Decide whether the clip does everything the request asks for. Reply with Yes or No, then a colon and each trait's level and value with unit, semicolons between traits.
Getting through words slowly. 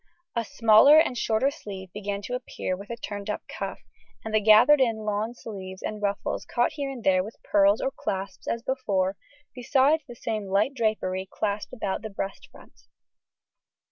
No: average, 175 wpm